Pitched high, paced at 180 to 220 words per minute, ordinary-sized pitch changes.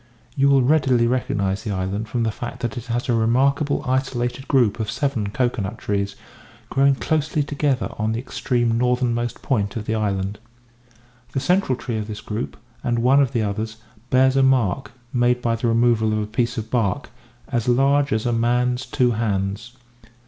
No: low, 120 Hz; average, 185 wpm; average, 3.1 semitones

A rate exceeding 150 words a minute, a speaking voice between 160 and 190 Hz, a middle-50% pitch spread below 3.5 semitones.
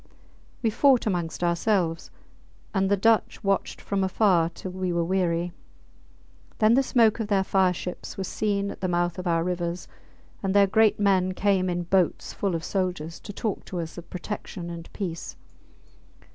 Yes: average, 175 wpm; medium, 185 Hz; narrow, 2.6 semitones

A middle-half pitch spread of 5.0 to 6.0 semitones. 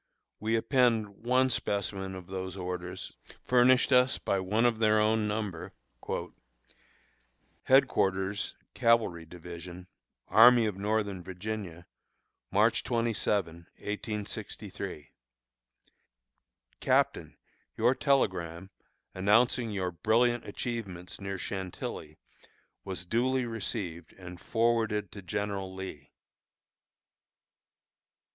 No: average, 3.9 semitones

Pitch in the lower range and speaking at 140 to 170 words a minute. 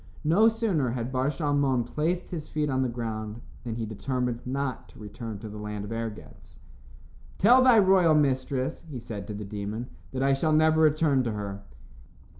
No: low, 130 Hz; average, 185 wpm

